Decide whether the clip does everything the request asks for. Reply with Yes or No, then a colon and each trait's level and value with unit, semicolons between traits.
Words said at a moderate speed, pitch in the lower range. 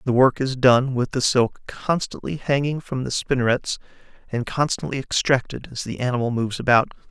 Yes: average, 170 wpm; low, 130 Hz